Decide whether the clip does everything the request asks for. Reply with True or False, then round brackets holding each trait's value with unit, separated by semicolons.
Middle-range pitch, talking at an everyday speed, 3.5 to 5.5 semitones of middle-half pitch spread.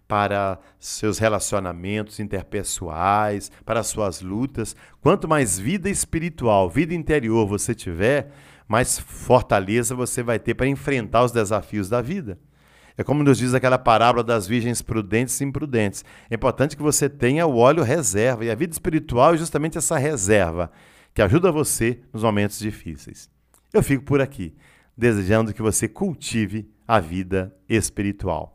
False (115 Hz; 145 wpm; 4.9 semitones)